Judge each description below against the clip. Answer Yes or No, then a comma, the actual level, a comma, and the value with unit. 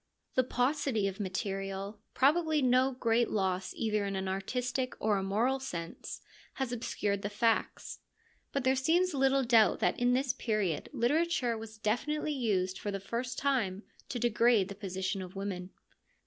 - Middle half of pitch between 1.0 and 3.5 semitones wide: No, average, 4.8 semitones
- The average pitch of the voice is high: Yes, high, 225 Hz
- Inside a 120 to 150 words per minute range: No, average, 160 wpm